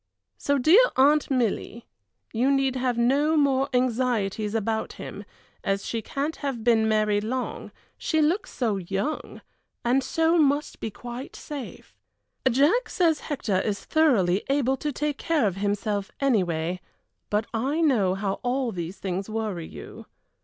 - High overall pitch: Yes, high, 245 Hz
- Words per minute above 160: No, average, 145 wpm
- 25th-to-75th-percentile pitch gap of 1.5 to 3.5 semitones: No, wide, 5.5 semitones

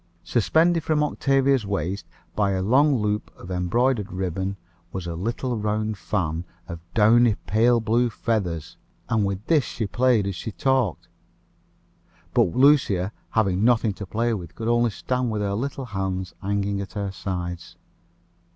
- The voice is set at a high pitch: No, low, 105 Hz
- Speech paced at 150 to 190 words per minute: Yes, average, 155 wpm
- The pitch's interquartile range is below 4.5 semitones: Yes, average, 4.0 semitones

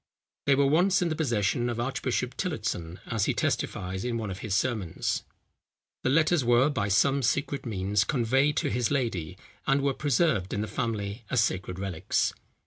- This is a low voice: Yes, low, 120 Hz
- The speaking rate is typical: Yes, average, 175 wpm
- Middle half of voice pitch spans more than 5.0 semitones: Yes, wide, 5.5 semitones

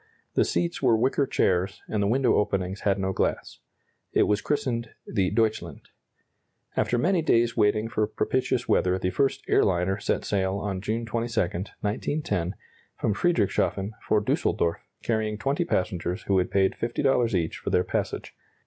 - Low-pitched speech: Yes, low, 105 Hz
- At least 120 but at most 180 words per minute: Yes, average, 160 wpm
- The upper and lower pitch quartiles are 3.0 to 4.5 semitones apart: Yes, average, 3.7 semitones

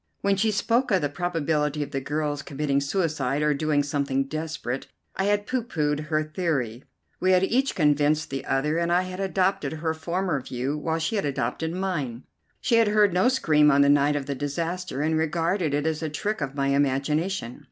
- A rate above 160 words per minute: Yes, average, 200 wpm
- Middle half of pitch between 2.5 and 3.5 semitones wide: No, average, 4.2 semitones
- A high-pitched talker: No, medium, 155 Hz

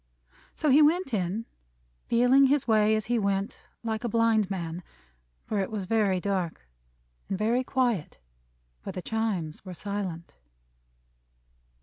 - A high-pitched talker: Yes, high, 215 Hz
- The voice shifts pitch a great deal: No, average, 3.8 semitones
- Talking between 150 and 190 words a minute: No, slow, 135 wpm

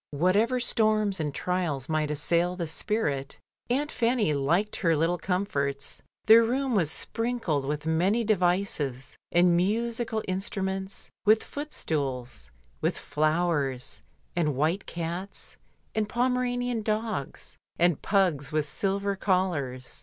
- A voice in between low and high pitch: Yes, medium, 180 Hz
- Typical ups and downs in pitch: No, wide, 6.1 semitones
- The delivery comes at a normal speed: No, slow, 120 wpm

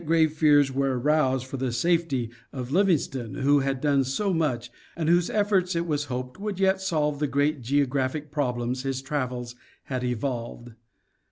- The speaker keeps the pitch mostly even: No, average, 3.7 semitones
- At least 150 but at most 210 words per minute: Yes, average, 165 wpm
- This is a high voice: No, medium, 140 Hz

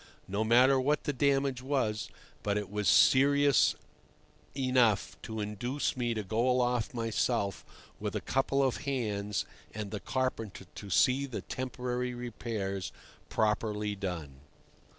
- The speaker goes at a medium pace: No, slow, 130 wpm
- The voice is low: Yes, low, 120 Hz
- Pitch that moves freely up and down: No, average, 3.8 semitones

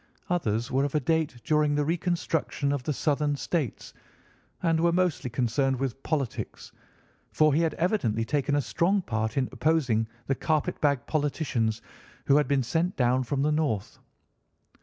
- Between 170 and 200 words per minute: No, average, 160 wpm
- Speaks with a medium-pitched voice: Yes, medium, 145 Hz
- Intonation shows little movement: No, average, 4.0 semitones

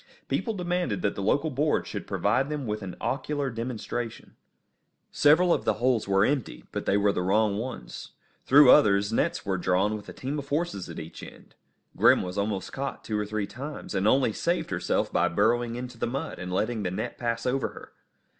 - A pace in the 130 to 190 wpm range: No, average, 200 wpm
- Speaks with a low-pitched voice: Yes, low, 115 Hz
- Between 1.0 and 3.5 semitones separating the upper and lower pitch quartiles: No, wide, 5.4 semitones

